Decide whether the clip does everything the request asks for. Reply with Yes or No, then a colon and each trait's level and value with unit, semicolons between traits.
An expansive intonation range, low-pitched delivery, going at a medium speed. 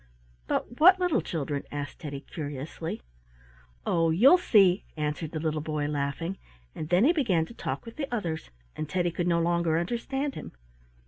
No: wide, 7.0 semitones; medium, 170 Hz; average, 170 wpm